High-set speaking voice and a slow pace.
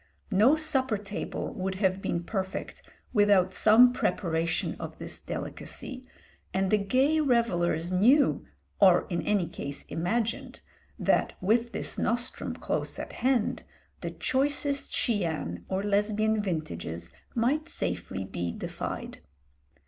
Yes: high, 205 Hz; slow, 120 wpm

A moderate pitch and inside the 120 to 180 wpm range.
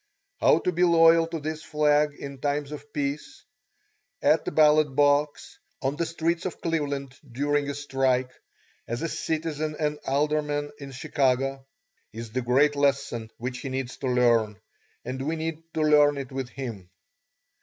Yes: medium, 145 Hz; average, 160 wpm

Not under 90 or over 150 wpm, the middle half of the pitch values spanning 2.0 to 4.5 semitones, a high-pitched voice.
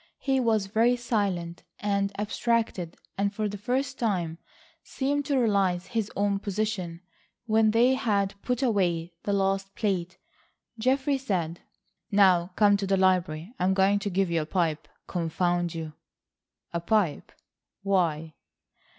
Yes: average, 140 wpm; average, 4.0 semitones; high, 195 Hz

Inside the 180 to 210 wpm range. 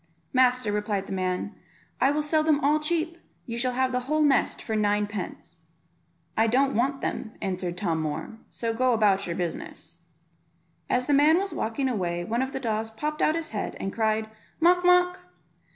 Yes: average, 185 wpm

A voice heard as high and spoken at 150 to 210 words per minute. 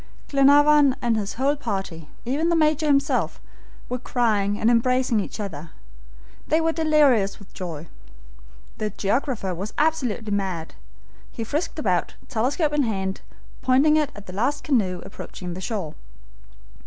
No: high, 235 Hz; average, 140 wpm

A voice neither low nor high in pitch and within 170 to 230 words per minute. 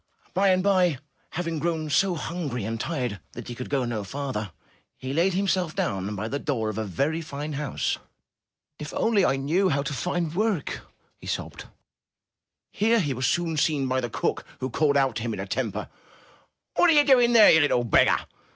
Yes: medium, 145 Hz; average, 195 wpm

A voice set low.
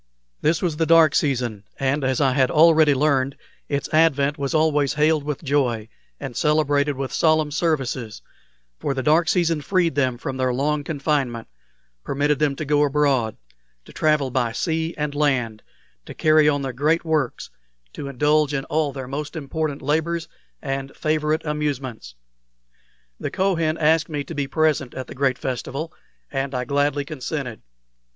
No: medium, 145 Hz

